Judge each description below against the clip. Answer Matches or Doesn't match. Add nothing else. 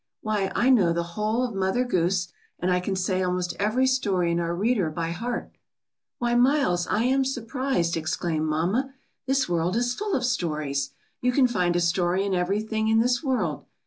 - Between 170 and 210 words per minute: Matches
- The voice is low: Doesn't match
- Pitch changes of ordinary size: Doesn't match